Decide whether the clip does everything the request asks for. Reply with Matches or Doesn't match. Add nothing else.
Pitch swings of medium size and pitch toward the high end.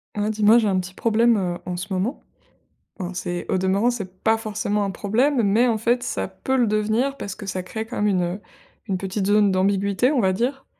Matches